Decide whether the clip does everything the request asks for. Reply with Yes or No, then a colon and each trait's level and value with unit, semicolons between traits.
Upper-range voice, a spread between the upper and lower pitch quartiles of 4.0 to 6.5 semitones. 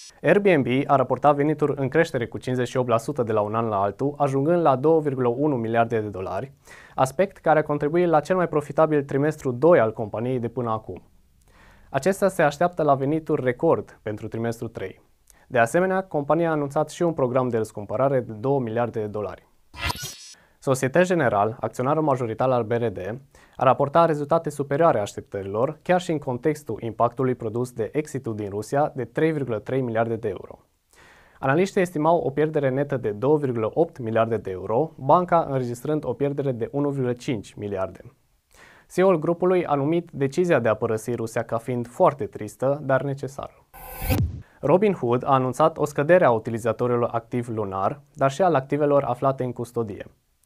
No: low, 135 Hz; average, 4.7 semitones